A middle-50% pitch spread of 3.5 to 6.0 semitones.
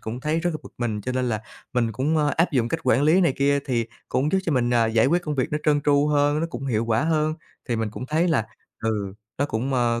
Yes: average, 4.6 semitones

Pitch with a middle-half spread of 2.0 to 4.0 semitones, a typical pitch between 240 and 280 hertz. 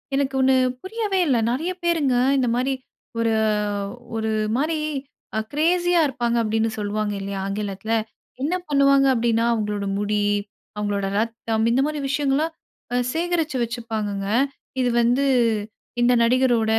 No: average, 4.4 semitones; high, 245 Hz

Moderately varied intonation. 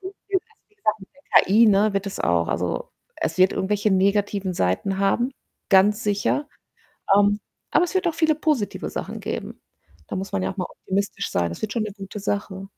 Yes: average, 3.0 semitones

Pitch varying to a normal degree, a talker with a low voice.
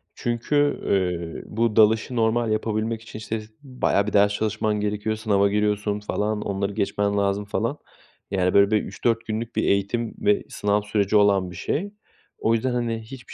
No: narrow, 1.9 semitones; low, 105 Hz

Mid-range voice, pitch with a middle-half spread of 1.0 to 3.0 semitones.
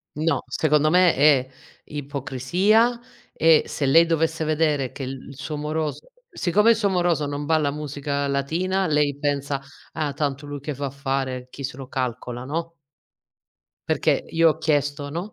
Yes: medium, 145 Hz; average, 2.7 semitones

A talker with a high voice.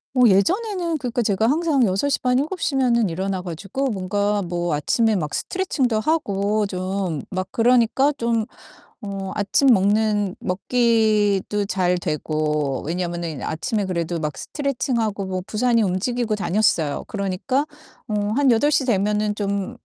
Yes: high, 210 Hz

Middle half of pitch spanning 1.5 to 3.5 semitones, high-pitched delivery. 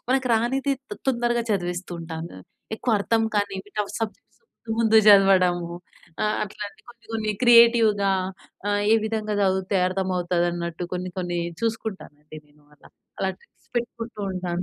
No: average, 4.0 semitones; high, 205 Hz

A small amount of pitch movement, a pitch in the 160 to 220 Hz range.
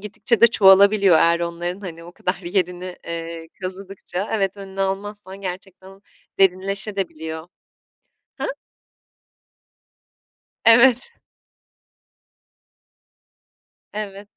Yes: narrow, 2.2 semitones; high, 190 Hz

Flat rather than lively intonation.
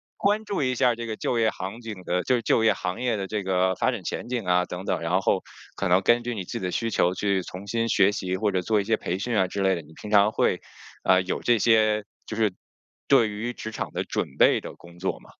No: average, 3.7 semitones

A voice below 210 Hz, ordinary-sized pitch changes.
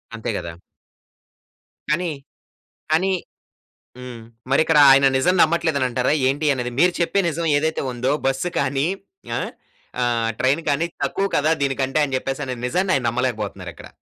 Yes: low, 135 Hz; average, 4.1 semitones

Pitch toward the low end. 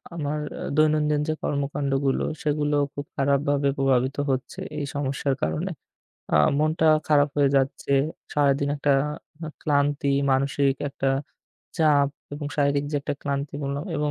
No: medium, 145 Hz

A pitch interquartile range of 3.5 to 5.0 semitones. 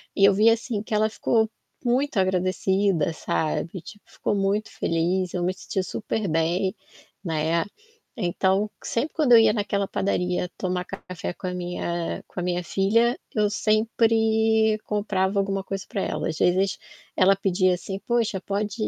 No: average, 3.1 semitones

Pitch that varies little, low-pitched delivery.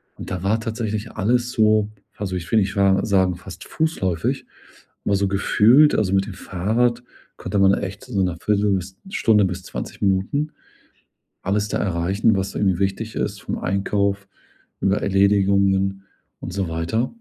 Yes: narrow, 2.1 semitones; low, 100 Hz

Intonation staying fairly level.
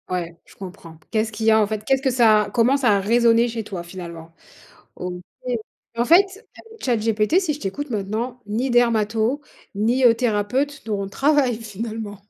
No: average, 3.5 semitones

